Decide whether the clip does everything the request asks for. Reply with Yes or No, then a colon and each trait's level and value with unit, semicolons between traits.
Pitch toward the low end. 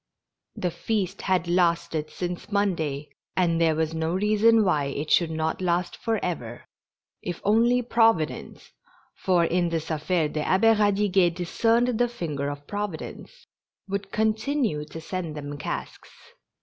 No: medium, 180 Hz